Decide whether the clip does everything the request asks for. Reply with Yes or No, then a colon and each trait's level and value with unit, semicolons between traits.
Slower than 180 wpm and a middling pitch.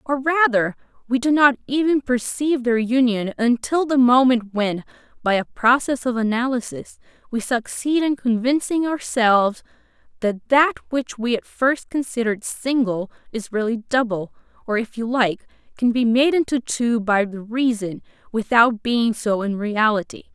No: average, 150 wpm; high, 240 Hz